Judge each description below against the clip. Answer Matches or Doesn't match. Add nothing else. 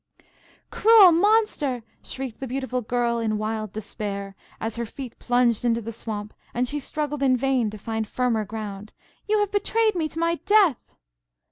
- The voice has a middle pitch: Doesn't match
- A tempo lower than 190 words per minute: Matches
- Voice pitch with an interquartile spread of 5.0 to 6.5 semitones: Matches